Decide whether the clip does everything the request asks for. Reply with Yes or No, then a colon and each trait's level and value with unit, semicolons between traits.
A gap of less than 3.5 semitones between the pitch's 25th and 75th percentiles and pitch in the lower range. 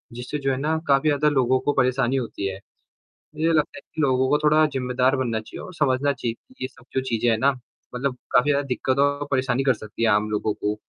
Yes: average, 2.7 semitones; low, 130 Hz